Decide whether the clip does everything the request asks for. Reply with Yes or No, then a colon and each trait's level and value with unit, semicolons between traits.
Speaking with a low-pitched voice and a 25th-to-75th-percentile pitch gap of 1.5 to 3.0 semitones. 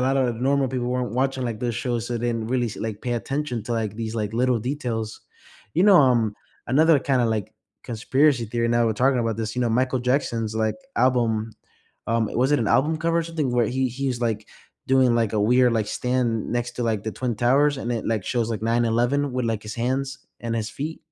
Yes: low, 120 Hz; narrow, 2.5 semitones